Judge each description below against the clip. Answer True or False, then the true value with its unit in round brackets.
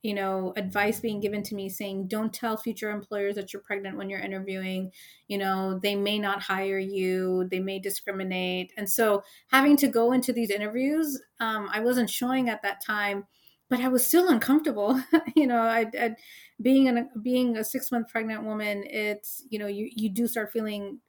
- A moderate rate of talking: True (195 wpm)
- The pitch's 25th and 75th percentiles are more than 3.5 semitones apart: False (3.1 semitones)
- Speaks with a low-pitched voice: False (215 Hz)